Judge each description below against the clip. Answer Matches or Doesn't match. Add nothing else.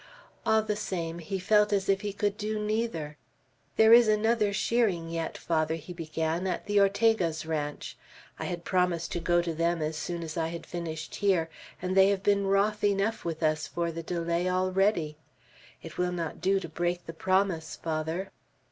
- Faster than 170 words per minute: Matches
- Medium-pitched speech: Matches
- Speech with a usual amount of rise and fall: Matches